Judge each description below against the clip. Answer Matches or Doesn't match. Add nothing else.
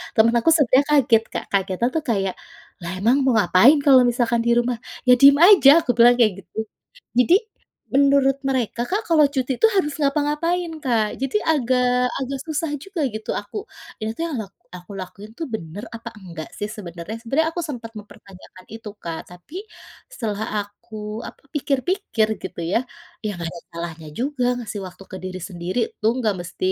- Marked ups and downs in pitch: Matches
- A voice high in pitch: Matches